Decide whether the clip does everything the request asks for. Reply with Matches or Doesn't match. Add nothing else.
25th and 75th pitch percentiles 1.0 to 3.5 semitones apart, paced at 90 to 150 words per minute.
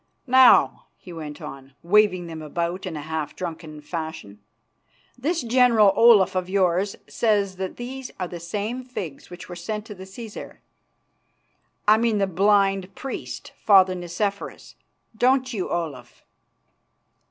Doesn't match